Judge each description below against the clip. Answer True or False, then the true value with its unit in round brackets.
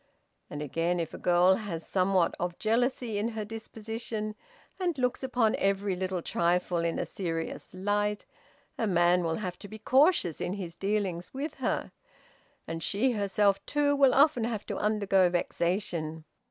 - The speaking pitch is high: True (200 Hz)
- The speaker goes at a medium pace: True (160 wpm)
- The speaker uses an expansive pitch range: False (4.1 semitones)